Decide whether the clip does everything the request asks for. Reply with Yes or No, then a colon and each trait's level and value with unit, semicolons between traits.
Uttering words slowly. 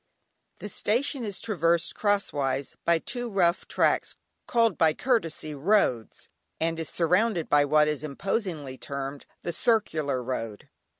Yes: slow, 130 wpm